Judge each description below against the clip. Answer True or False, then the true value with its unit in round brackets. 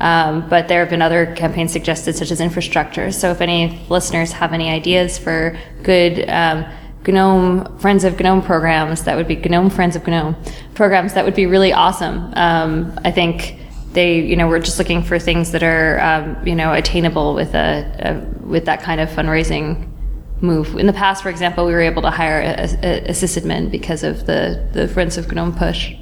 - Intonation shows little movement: True (1.6 semitones)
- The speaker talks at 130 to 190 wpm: False (200 wpm)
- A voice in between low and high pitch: True (170 Hz)